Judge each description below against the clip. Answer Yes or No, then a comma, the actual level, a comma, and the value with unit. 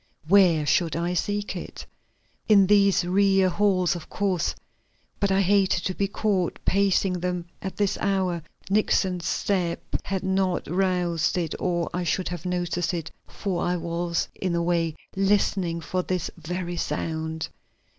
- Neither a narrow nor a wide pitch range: No, narrow, 2.1 semitones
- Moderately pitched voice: Yes, medium, 180 Hz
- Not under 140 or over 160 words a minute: Yes, average, 150 wpm